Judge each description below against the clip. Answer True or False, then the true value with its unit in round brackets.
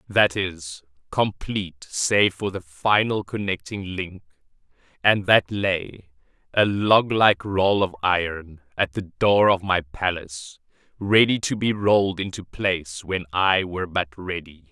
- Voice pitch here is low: True (95 Hz)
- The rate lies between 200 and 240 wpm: False (140 wpm)